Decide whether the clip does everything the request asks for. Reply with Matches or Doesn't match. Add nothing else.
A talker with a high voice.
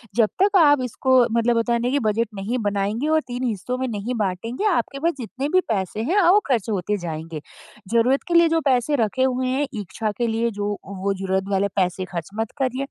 Matches